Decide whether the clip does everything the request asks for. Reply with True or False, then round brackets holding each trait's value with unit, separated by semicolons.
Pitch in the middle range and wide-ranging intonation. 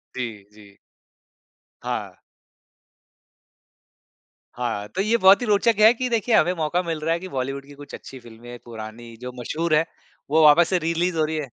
True (155 Hz; 6.8 semitones)